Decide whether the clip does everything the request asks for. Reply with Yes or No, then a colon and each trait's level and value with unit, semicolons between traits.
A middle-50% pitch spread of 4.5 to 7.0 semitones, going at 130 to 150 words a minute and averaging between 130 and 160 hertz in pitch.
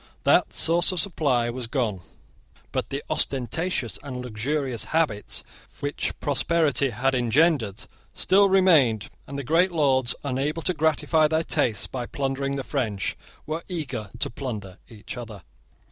Yes: average, 4.9 semitones; average, 140 wpm; low, 135 Hz